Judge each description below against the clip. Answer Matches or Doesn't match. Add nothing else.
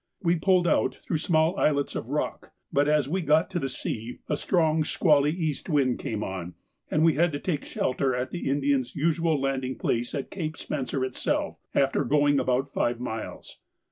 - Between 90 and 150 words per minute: Doesn't match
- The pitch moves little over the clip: Doesn't match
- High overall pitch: Doesn't match